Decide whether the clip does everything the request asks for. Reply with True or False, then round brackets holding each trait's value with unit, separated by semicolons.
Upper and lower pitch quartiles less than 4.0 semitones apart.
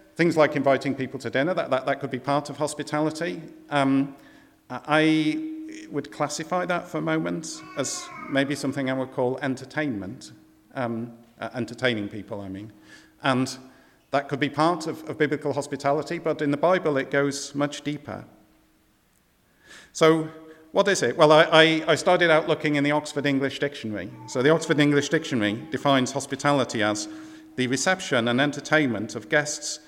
True (3.2 semitones)